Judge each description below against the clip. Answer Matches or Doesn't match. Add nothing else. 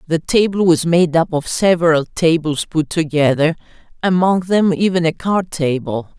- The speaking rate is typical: Matches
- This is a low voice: Doesn't match